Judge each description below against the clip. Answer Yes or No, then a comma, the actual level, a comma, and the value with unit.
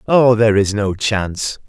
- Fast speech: No, average, 180 wpm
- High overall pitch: No, low, 110 Hz